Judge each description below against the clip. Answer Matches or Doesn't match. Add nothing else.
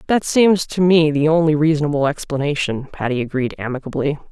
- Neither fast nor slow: Matches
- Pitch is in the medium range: Matches